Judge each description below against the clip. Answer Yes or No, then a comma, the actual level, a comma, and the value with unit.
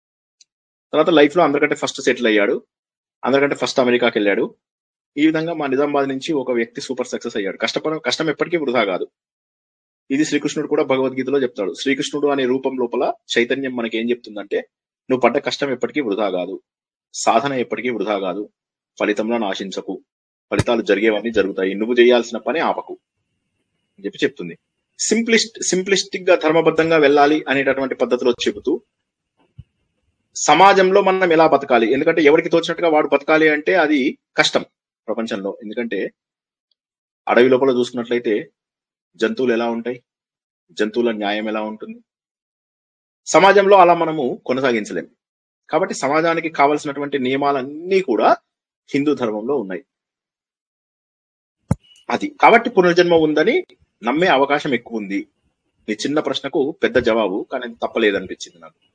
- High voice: No, medium, 140 Hz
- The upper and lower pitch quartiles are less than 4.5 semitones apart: No, average, 5.1 semitones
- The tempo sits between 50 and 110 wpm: No, fast, 125 wpm